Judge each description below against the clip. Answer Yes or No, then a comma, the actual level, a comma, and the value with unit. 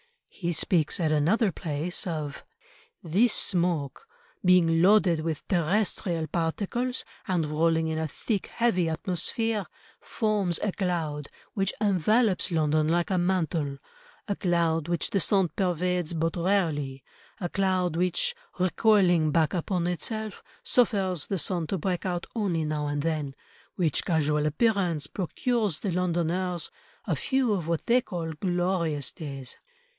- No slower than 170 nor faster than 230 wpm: No, slow, 135 wpm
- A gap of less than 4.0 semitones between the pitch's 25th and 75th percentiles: Yes, average, 3.4 semitones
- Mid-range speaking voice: Yes, medium, 175 Hz